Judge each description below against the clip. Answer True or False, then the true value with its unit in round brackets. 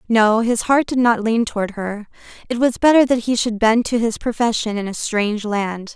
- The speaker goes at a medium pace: False (220 wpm)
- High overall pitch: True (225 Hz)